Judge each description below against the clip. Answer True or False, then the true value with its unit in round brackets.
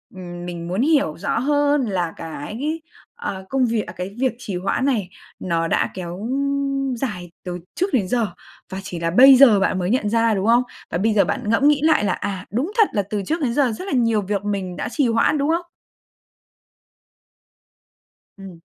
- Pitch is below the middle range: False (215 Hz)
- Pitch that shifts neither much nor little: False (6.4 semitones)